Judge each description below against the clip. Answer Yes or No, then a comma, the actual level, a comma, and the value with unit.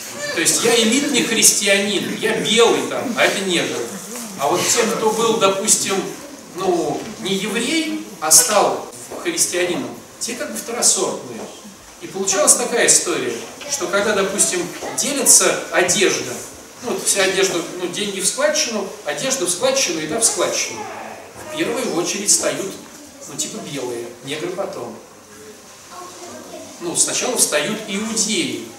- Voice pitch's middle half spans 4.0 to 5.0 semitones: No, average, 3.5 semitones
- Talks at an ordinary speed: Yes, average, 130 wpm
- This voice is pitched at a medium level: No, high, 210 Hz